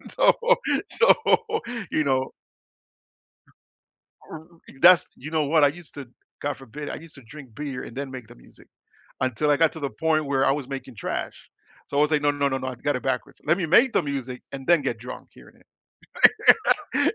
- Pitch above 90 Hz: Yes, medium, 140 Hz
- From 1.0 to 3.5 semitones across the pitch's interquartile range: Yes, average, 2.9 semitones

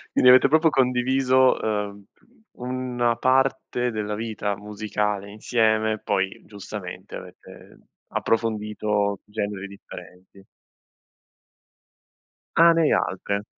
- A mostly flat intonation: No, average, 3.7 semitones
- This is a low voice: Yes, low, 110 Hz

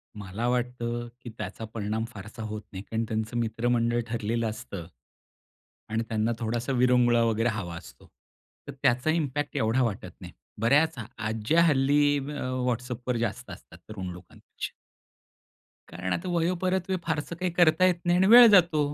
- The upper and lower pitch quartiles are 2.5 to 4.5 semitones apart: No, average, 5.1 semitones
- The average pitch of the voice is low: Yes, low, 120 Hz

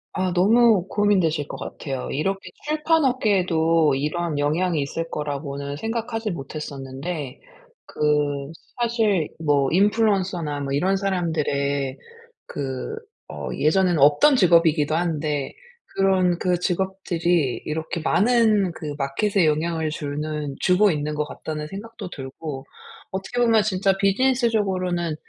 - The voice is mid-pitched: Yes, medium, 170 Hz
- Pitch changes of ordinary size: Yes, average, 4.8 semitones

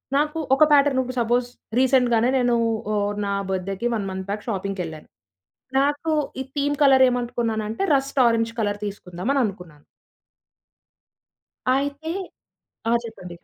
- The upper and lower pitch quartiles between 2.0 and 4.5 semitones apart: No, average, 5.1 semitones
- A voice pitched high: Yes, high, 230 Hz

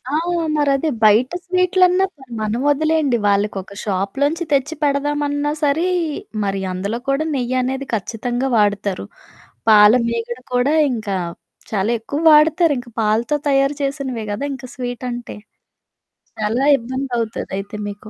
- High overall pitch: Yes, very high, 250 Hz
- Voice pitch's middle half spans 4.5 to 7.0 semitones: Yes, average, 5.0 semitones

